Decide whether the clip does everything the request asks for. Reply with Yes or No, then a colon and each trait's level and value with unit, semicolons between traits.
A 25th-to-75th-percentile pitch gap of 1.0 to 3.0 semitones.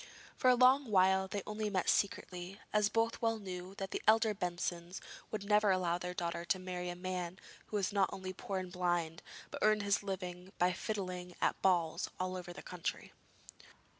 Yes: narrow, 2.4 semitones